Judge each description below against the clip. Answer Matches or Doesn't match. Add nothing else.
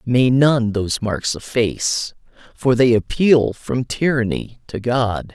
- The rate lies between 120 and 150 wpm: Matches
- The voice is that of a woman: Doesn't match